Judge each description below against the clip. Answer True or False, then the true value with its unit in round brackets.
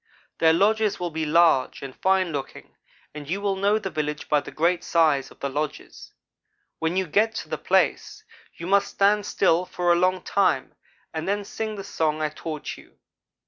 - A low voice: False (175 Hz)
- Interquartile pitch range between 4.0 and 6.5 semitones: True (4.3 semitones)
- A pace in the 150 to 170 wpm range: False (190 wpm)